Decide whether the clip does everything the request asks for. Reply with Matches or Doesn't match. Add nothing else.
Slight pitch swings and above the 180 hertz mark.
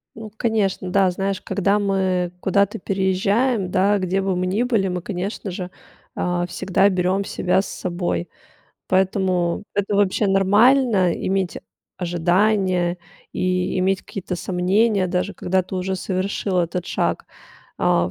Matches